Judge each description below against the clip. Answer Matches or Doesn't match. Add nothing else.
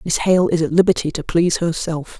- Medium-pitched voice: Matches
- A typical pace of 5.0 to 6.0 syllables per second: Matches